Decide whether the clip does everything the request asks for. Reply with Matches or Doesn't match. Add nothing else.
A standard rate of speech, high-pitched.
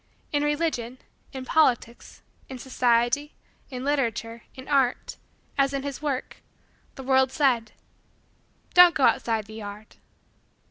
Doesn't match